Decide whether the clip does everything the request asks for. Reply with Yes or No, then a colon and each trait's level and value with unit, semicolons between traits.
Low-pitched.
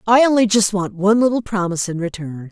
No: high, 200 Hz